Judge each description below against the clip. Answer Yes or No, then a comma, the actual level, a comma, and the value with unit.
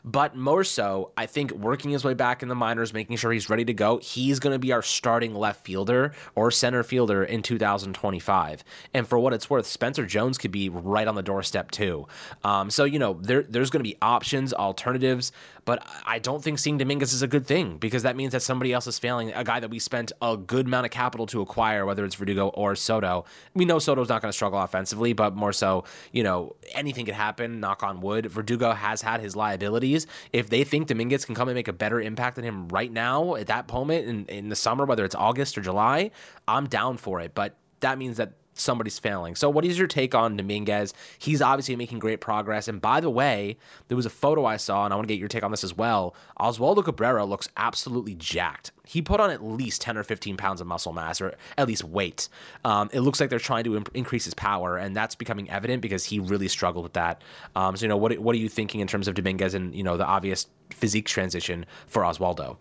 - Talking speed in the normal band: No, fast, 240 wpm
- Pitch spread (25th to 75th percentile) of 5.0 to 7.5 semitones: No, average, 3.9 semitones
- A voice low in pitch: Yes, low, 115 Hz